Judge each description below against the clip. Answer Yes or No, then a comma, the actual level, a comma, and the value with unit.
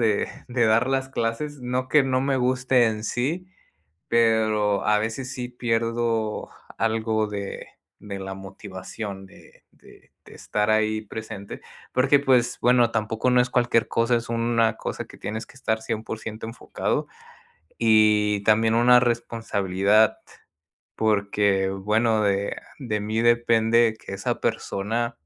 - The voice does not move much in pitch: Yes, narrow, 2.2 semitones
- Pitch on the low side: Yes, low, 115 Hz